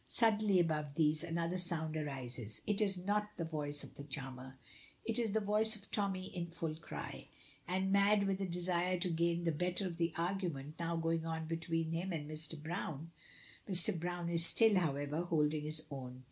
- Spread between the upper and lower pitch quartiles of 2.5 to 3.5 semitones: Yes, average, 3.2 semitones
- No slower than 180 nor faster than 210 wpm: Yes, average, 190 wpm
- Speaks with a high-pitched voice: No, medium, 170 Hz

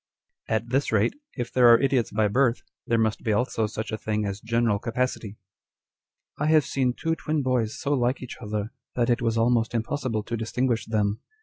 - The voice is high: No, low, 115 Hz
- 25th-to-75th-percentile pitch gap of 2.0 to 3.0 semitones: Yes, narrow, 2.6 semitones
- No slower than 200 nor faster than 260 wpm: Yes, fast, 205 wpm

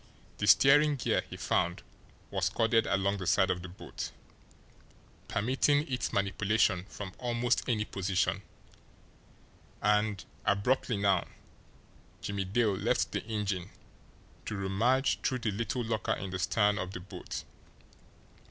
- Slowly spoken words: Yes, slow, 130 wpm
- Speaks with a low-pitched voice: Yes, low, 105 Hz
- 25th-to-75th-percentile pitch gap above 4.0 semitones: No, average, 3.6 semitones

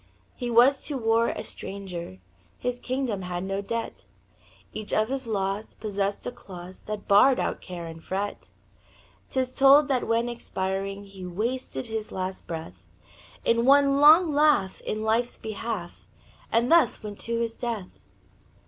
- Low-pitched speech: No, high, 220 Hz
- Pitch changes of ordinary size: Yes, average, 4.3 semitones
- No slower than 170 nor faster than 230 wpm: No, average, 150 wpm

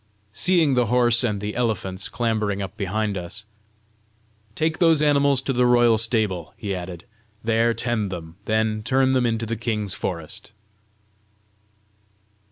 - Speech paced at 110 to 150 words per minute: Yes, average, 140 wpm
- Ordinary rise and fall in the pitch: Yes, average, 3.5 semitones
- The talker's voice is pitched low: Yes, low, 110 Hz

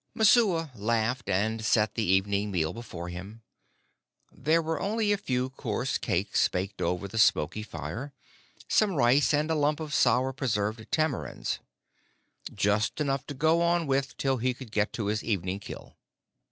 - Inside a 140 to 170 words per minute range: Yes, average, 160 wpm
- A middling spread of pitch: No, wide, 6.3 semitones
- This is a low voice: Yes, low, 120 Hz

